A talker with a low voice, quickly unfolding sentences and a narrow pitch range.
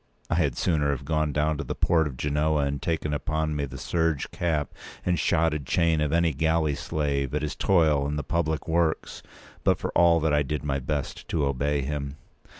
Yes: very low, 75 Hz; fast, 210 wpm; narrow, 2.0 semitones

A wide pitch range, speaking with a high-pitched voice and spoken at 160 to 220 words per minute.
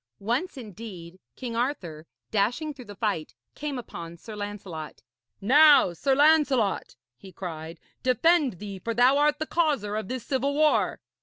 No: wide, 6.6 semitones; high, 230 Hz; average, 150 wpm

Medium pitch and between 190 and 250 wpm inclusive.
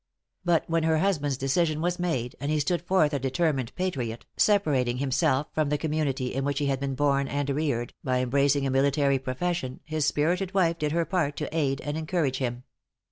Yes: medium, 145 Hz; average, 195 wpm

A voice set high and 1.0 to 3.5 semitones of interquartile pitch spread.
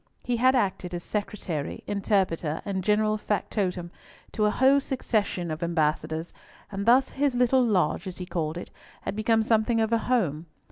No: high, 205 Hz; average, 4.8 semitones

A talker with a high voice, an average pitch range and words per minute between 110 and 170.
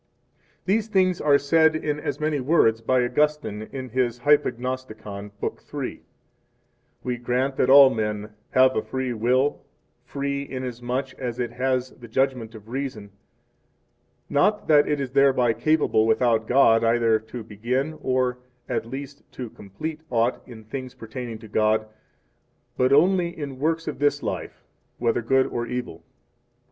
No: low, 130 Hz; average, 3.6 semitones; average, 150 wpm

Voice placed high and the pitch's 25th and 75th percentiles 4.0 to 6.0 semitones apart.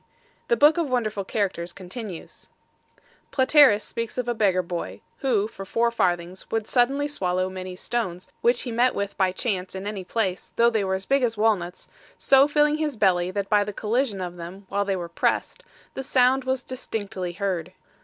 Yes: high, 210 Hz; average, 5.0 semitones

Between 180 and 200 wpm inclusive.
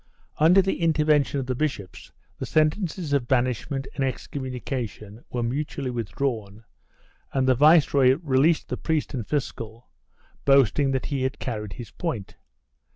No: average, 150 wpm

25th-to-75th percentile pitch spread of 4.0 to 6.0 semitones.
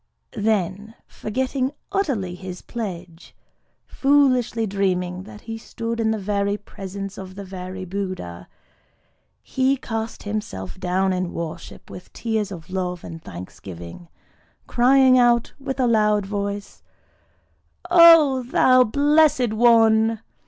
Yes: average, 4.7 semitones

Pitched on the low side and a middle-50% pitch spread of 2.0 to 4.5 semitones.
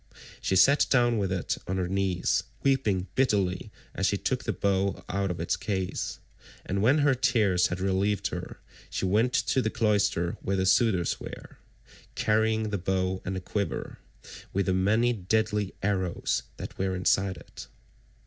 Yes: low, 100 Hz; average, 2.9 semitones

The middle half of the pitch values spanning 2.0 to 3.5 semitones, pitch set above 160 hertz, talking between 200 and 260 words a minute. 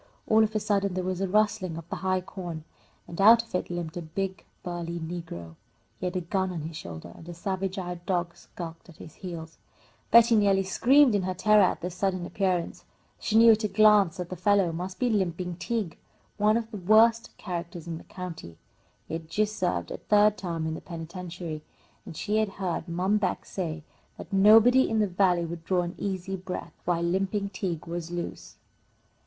Yes: average, 3.2 semitones; medium, 185 Hz; fast, 205 wpm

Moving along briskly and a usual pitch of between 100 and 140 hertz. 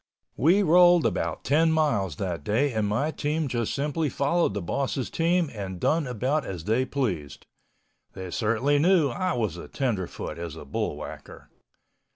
No: average, 160 wpm; low, 135 Hz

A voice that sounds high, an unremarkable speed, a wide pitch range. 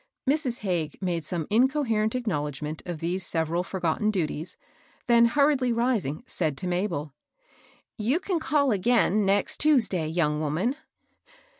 Yes: high, 195 Hz; average, 145 wpm; wide, 7.0 semitones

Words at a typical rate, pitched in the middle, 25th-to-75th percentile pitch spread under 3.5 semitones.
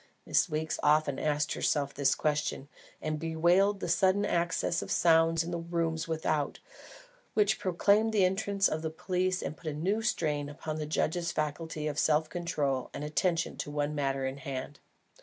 Yes: average, 175 wpm; medium, 160 Hz; average, 2.9 semitones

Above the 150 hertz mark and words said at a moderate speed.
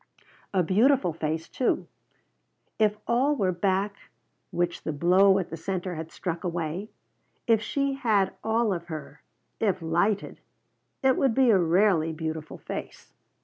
Yes: high, 190 Hz; average, 145 wpm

